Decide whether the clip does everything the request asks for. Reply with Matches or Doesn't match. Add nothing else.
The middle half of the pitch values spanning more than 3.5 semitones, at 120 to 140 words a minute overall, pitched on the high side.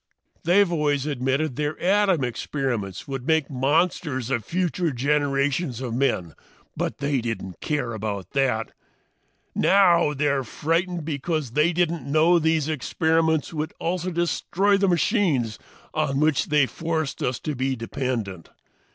Doesn't match